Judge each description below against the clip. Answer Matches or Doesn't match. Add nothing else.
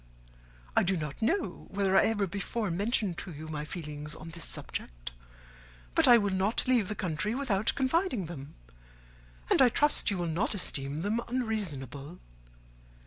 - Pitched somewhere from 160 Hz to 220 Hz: Matches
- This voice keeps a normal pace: Matches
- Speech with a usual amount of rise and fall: Doesn't match